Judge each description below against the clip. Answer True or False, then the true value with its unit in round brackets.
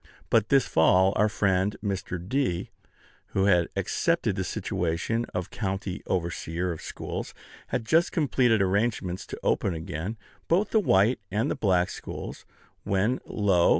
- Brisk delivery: False (145 wpm)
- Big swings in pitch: False (4.0 semitones)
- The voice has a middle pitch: False (95 Hz)